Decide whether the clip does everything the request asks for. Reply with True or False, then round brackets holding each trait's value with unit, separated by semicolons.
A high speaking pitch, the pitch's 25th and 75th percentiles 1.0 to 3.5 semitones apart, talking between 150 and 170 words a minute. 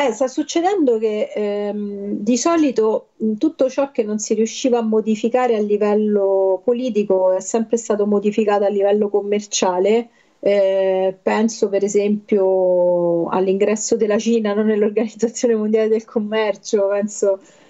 False (215 Hz; 2.5 semitones; 130 wpm)